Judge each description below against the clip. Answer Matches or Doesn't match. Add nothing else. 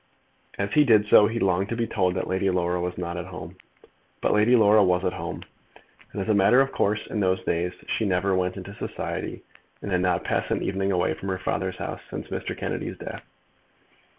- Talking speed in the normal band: Doesn't match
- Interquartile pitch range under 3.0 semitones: Matches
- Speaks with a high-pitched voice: Doesn't match